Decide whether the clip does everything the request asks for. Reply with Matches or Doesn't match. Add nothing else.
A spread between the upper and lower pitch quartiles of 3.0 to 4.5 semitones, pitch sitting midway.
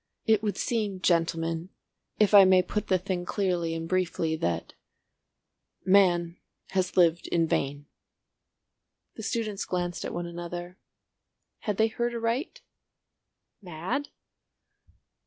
Matches